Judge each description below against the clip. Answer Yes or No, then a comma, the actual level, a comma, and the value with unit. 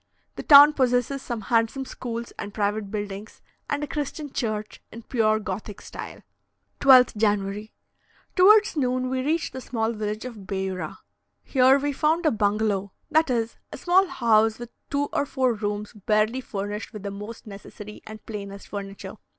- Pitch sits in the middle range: No, high, 225 Hz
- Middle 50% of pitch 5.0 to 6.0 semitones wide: No, average, 4.1 semitones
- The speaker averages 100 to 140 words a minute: No, average, 160 wpm